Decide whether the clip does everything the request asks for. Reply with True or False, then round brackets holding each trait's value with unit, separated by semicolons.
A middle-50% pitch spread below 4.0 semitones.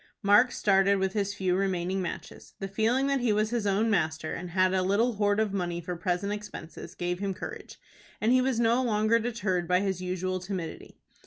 True (3.0 semitones)